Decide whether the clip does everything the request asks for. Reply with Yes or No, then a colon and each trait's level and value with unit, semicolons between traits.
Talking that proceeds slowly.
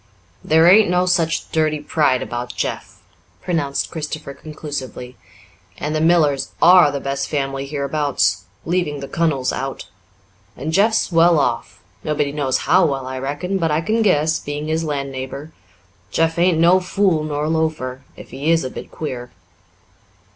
No: average, 155 wpm